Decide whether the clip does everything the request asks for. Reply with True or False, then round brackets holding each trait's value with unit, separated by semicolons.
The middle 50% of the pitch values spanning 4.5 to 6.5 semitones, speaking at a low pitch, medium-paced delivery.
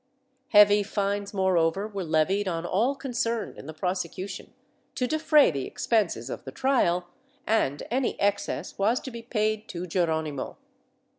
False (4.8 semitones; 200 Hz; 150 wpm)